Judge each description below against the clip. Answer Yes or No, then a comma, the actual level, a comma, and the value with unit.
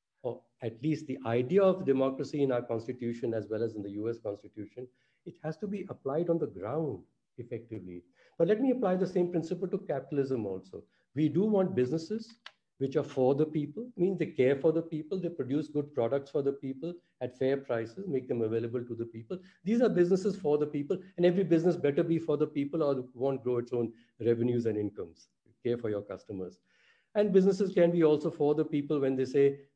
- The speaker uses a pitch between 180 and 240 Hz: No, medium, 140 Hz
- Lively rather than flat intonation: Yes, wide, 6.1 semitones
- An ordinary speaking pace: No, fast, 210 wpm